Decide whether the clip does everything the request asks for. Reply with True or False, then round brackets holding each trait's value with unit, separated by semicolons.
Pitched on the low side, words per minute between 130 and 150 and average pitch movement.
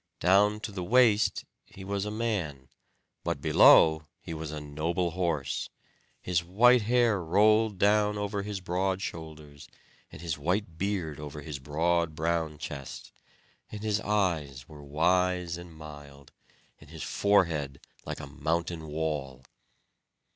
True (85 Hz; 140 wpm; 5.0 semitones)